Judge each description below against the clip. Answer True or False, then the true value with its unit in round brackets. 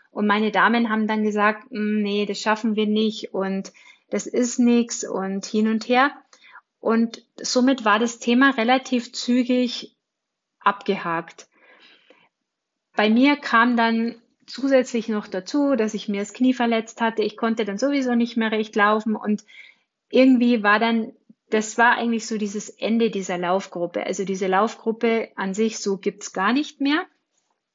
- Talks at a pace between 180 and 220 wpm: False (155 wpm)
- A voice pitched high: True (225 Hz)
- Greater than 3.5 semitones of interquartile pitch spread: False (2.7 semitones)